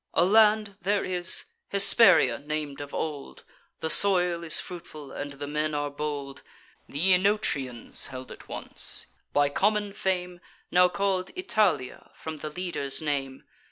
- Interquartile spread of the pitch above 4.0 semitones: Yes, average, 4.9 semitones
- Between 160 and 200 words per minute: No, average, 140 wpm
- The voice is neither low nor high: Yes, medium, 170 Hz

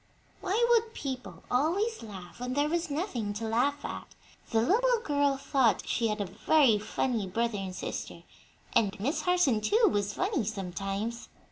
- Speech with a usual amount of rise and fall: No, wide, 7.1 semitones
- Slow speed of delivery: No, average, 160 wpm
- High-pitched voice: Yes, very high, 250 Hz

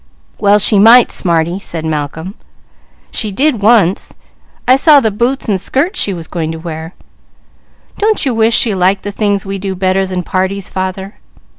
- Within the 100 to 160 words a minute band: No, average, 170 wpm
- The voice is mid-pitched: No, high, 195 Hz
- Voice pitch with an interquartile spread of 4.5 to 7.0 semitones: No, average, 3.5 semitones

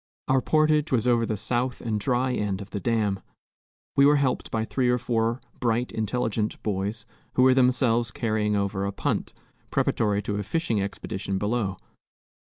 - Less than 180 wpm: Yes, average, 170 wpm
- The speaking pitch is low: Yes, low, 115 Hz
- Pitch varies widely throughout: No, average, 3.4 semitones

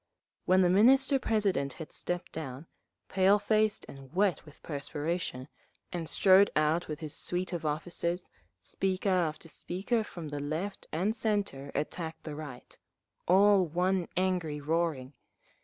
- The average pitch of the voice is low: No, medium, 175 Hz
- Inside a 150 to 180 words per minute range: No, average, 140 wpm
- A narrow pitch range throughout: No, average, 4.1 semitones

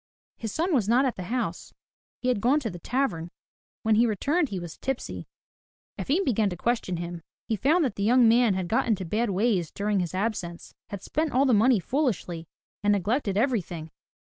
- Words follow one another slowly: No, average, 195 wpm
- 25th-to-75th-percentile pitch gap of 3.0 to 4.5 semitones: No, wide, 5.4 semitones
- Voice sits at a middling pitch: No, high, 220 Hz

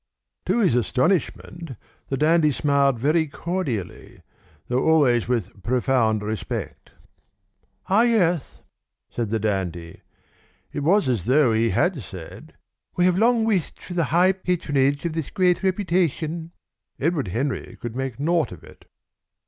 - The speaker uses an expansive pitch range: Yes, wide, 6.4 semitones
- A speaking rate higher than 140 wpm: No, slow, 135 wpm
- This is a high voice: No, medium, 145 Hz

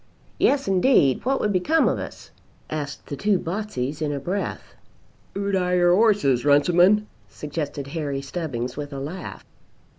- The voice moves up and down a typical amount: No, wide, 5.8 semitones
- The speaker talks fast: No, average, 150 wpm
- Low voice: No, medium, 170 Hz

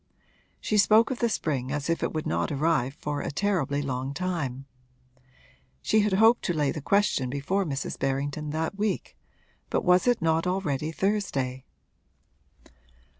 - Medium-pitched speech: Yes, medium, 155 Hz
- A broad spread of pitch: Yes, wide, 6.0 semitones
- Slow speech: No, average, 155 wpm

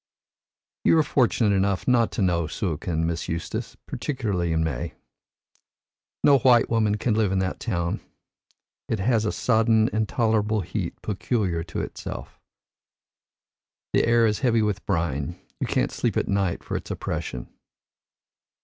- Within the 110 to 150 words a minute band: Yes, average, 140 wpm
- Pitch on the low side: Yes, low, 105 Hz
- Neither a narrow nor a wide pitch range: Yes, average, 4.8 semitones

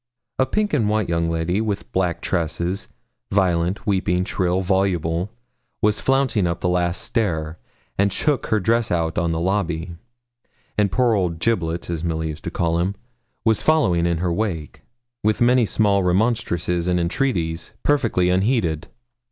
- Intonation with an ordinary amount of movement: Yes, average, 4.2 semitones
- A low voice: Yes, very low, 90 Hz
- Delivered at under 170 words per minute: Yes, average, 155 wpm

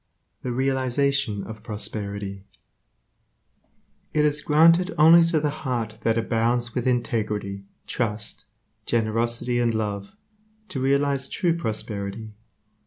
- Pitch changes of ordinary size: Yes, average, 4.4 semitones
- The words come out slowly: Yes, slow, 110 wpm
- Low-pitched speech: Yes, low, 120 Hz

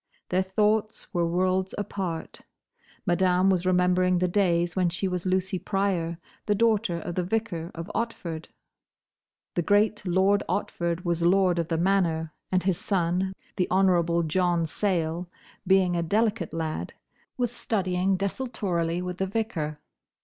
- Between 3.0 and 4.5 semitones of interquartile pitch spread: No, narrow, 2.4 semitones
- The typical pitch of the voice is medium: Yes, medium, 180 Hz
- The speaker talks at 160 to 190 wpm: No, average, 140 wpm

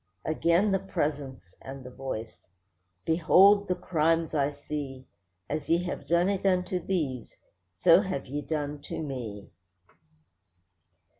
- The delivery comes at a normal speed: No, slow, 130 wpm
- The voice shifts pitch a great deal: No, average, 4.8 semitones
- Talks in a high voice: No, medium, 150 Hz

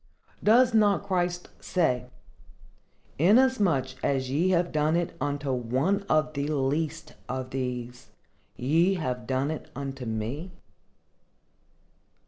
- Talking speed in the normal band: No, slow, 110 wpm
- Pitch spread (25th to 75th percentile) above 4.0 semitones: Yes, average, 5.2 semitones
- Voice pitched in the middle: Yes, medium, 150 Hz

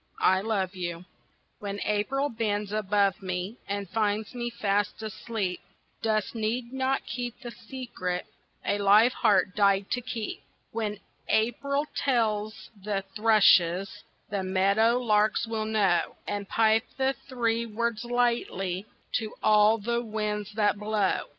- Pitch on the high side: Yes, high, 215 Hz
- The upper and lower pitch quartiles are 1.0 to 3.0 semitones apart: Yes, narrow, 2.6 semitones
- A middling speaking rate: No, slow, 130 wpm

